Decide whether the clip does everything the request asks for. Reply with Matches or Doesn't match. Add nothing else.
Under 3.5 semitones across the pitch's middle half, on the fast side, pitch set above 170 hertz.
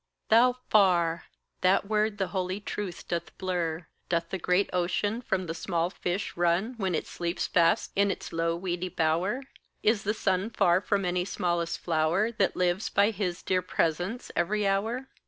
Doesn't match